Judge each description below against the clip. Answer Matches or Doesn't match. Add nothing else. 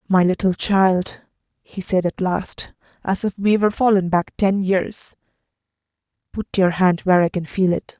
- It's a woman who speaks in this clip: Matches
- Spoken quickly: Doesn't match